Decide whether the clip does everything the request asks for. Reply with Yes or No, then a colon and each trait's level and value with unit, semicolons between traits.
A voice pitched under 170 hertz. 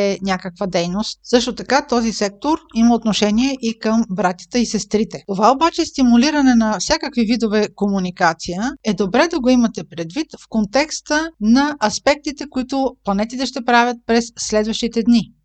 No: high, 230 Hz